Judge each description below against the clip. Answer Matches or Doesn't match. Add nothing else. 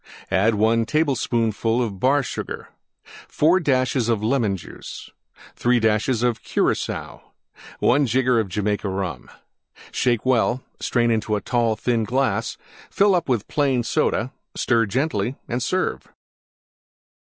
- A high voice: Doesn't match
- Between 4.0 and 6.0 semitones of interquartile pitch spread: Doesn't match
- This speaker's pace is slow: Matches